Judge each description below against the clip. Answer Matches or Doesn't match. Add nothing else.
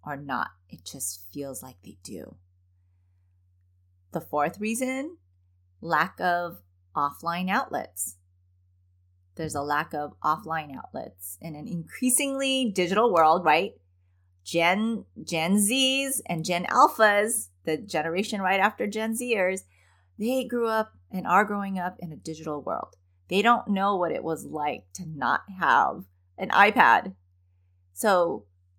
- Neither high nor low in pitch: Matches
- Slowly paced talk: Matches